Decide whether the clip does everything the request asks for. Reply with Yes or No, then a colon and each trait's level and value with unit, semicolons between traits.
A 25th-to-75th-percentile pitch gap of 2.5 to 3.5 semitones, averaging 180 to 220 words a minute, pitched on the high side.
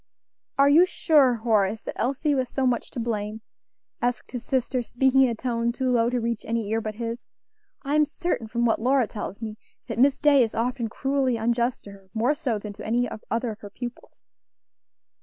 Yes: average, 2.8 semitones; fast, 205 wpm; high, 240 Hz